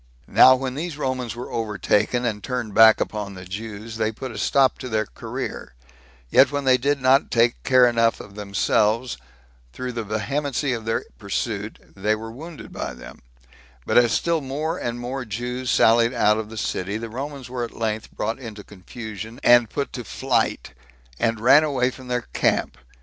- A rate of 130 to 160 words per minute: No, average, 180 wpm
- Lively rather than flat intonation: No, average, 3.1 semitones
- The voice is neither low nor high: No, low, 115 Hz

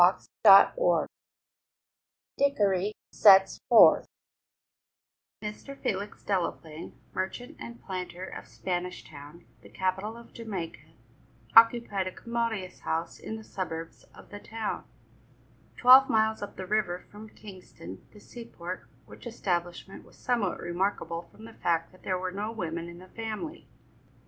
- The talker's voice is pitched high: Yes, high, 195 Hz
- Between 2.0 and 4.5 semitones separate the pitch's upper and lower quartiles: Yes, average, 3.8 semitones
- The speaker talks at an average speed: No, slow, 130 wpm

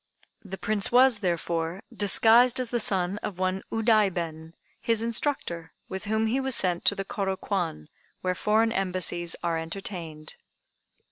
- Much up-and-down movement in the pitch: No, average, 4.4 semitones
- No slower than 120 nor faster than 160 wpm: Yes, average, 145 wpm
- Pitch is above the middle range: Yes, high, 195 Hz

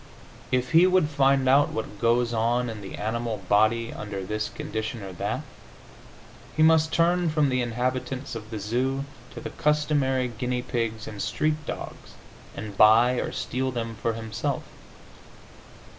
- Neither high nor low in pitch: No, low, 120 Hz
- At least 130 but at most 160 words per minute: Yes, average, 155 wpm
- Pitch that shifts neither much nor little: Yes, average, 3.7 semitones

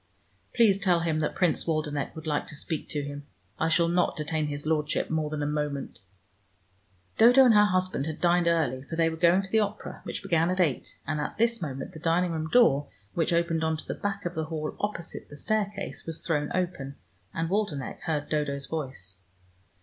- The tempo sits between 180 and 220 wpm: Yes, fast, 205 wpm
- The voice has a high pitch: No, medium, 160 Hz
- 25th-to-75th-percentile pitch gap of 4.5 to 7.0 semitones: No, average, 3.4 semitones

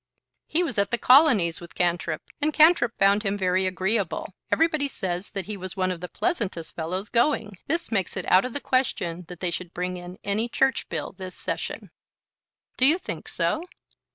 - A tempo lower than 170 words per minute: No, average, 190 wpm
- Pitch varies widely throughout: Yes, wide, 5.9 semitones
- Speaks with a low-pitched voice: No, high, 195 Hz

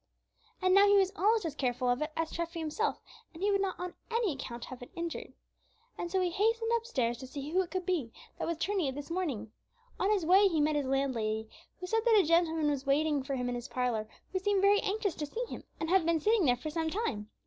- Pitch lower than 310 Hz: No, very high, 330 Hz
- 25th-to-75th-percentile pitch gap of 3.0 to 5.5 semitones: No, wide, 6.3 semitones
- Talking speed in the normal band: No, fast, 250 wpm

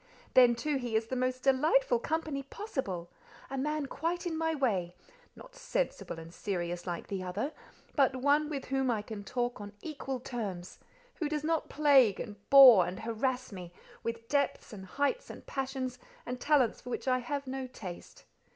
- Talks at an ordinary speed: Yes, average, 170 wpm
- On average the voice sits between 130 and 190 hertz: No, very high, 255 Hz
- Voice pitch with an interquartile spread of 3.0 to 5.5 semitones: Yes, average, 5.0 semitones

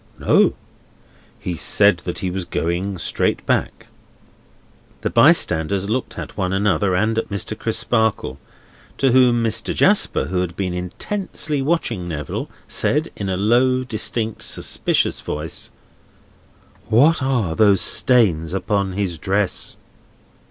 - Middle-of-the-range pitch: No, low, 100 Hz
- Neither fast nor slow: No, slow, 125 wpm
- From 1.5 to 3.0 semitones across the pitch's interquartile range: No, average, 4.8 semitones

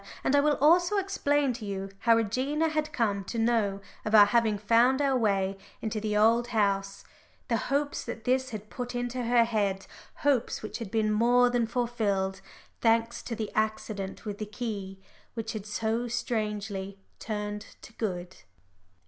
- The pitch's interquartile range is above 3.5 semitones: No, average, 3.0 semitones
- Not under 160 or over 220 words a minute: Yes, average, 165 wpm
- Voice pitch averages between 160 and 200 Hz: No, high, 225 Hz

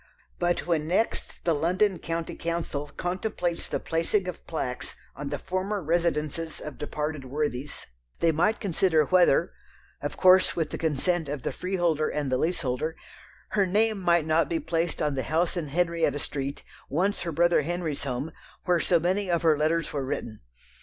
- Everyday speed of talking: Yes, average, 170 wpm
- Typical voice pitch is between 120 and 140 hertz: No, medium, 165 Hz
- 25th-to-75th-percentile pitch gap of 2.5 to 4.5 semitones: Yes, average, 2.9 semitones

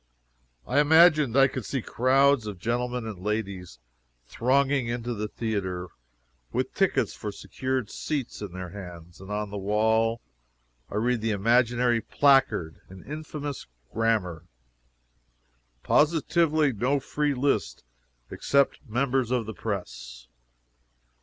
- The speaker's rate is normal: No, slow, 120 wpm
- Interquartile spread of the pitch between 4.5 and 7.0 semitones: Yes, average, 5.0 semitones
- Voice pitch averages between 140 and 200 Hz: No, low, 115 Hz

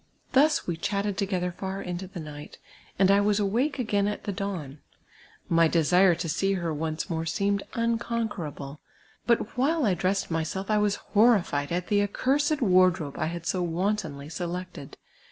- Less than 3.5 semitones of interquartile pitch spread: No, average, 3.8 semitones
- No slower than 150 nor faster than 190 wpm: Yes, average, 165 wpm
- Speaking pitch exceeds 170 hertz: Yes, high, 190 Hz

